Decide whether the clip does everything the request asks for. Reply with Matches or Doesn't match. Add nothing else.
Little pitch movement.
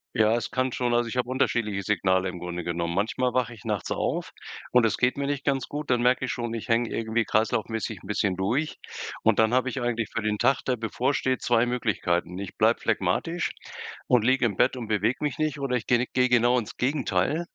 Doesn't match